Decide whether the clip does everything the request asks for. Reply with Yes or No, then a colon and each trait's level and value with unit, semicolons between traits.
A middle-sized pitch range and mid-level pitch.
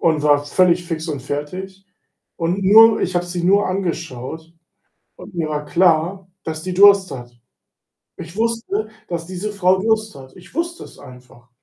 Yes: average, 3.9 semitones; medium, 175 Hz